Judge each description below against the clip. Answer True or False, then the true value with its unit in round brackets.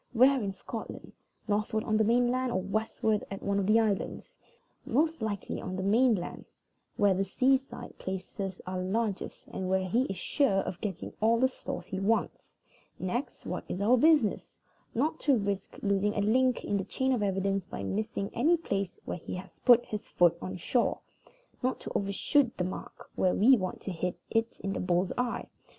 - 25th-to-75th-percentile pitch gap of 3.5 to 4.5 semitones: True (4.2 semitones)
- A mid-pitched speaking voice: False (205 Hz)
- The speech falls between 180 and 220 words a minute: True (190 wpm)